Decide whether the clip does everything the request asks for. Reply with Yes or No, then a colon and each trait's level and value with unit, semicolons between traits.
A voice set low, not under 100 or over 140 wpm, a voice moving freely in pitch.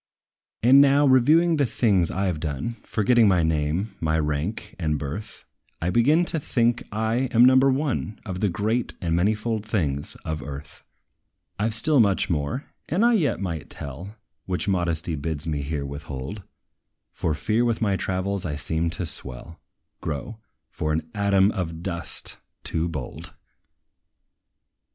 No: very low, 95 Hz; average, 155 wpm; wide, 6.5 semitones